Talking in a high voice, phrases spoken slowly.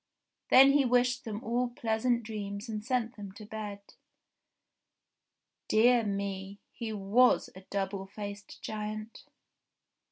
Yes: high, 215 Hz; slow, 120 wpm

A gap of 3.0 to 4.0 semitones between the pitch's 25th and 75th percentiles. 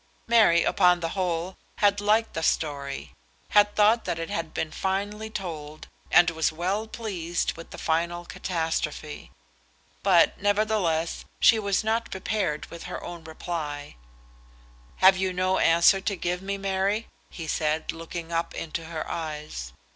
Yes: average, 3.6 semitones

